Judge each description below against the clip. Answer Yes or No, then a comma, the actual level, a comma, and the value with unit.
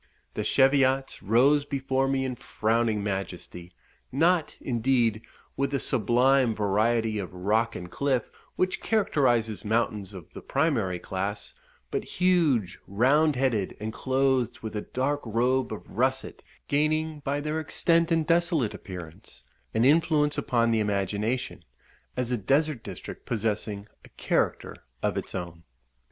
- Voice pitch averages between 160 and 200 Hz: No, low, 125 Hz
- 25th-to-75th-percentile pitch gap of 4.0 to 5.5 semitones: Yes, average, 5.0 semitones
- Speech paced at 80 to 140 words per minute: Yes, slow, 135 wpm